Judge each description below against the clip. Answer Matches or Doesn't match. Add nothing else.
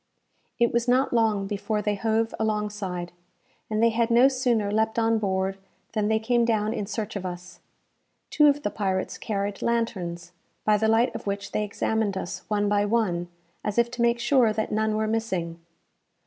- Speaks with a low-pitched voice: Doesn't match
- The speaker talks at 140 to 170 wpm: Doesn't match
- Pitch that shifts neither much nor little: Doesn't match